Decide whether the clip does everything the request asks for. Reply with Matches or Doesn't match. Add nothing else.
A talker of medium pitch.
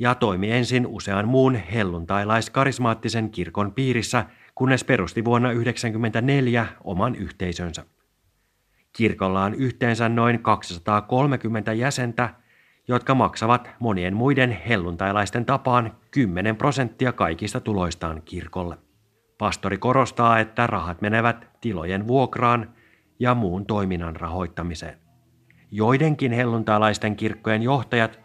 Doesn't match